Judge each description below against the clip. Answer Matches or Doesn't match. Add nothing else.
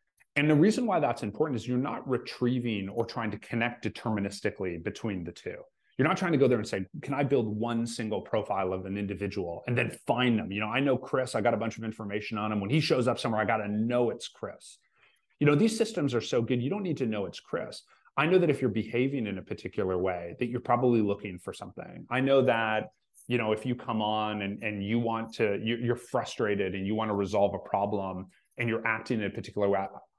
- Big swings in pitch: Doesn't match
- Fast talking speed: Matches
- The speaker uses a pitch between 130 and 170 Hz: Doesn't match